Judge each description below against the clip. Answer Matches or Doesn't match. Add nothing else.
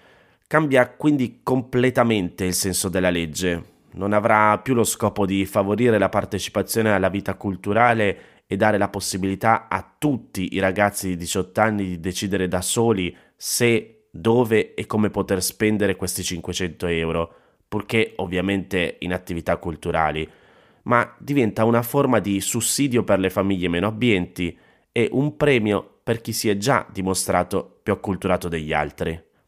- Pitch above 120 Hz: Doesn't match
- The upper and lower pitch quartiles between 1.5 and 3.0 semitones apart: Doesn't match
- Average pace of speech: Matches